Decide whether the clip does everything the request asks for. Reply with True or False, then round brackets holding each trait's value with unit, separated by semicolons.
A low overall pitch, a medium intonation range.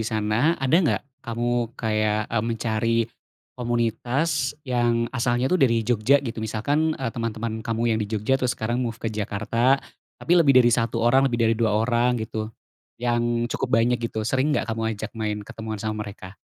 False (115 Hz; 2.0 semitones)